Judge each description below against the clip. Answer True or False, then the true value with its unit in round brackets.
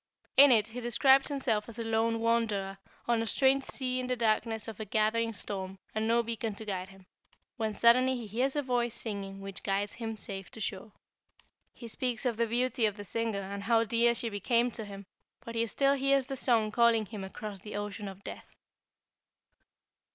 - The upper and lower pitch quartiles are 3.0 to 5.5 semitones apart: False (2.5 semitones)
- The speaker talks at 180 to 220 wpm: True (200 wpm)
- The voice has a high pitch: True (225 Hz)